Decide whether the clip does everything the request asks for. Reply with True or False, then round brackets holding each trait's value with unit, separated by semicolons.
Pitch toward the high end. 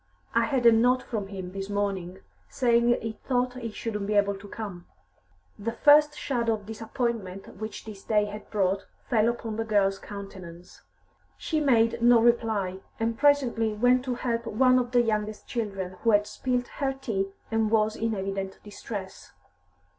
True (220 Hz)